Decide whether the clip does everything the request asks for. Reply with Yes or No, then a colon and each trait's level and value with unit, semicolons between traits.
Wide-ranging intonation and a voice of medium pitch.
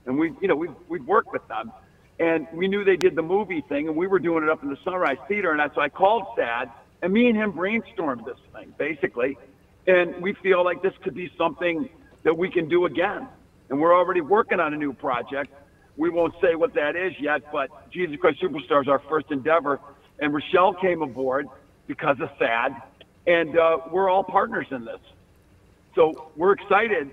No: average, 4.6 semitones; medium, 175 Hz